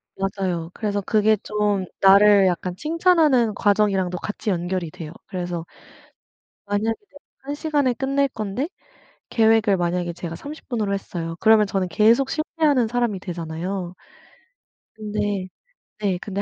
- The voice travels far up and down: No, average, 3.9 semitones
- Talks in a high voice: Yes, high, 205 Hz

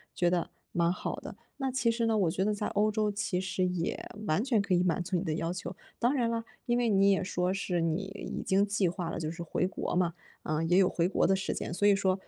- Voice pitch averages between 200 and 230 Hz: No, high, 190 Hz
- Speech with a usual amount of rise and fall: Yes, average, 3.0 semitones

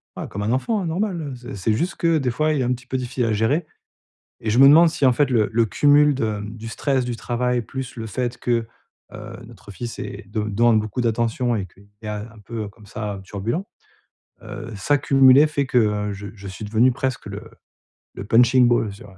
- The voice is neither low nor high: No, low, 120 Hz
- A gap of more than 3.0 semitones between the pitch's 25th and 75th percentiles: Yes, average, 3.7 semitones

